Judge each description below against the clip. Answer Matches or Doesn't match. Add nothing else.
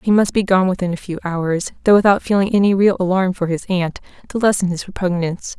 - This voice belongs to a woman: Matches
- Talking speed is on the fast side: Matches